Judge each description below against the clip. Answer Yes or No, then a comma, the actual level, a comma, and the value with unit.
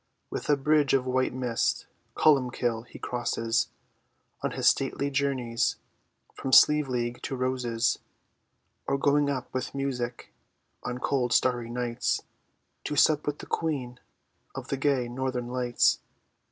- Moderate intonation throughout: No, narrow, 2.3 semitones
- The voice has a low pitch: Yes, low, 130 Hz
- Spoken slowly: Yes, slow, 130 wpm